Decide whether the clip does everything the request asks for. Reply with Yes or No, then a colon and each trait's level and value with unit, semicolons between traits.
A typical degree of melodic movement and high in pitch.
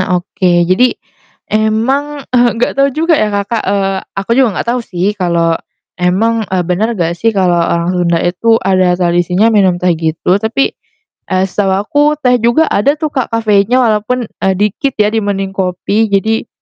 Yes: average, 4.1 semitones; high, 205 Hz